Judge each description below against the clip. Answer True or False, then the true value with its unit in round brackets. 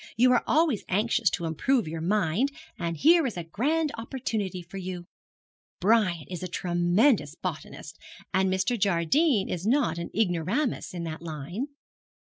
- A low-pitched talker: False (190 Hz)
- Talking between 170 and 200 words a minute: False (150 wpm)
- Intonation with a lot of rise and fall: True (6.1 semitones)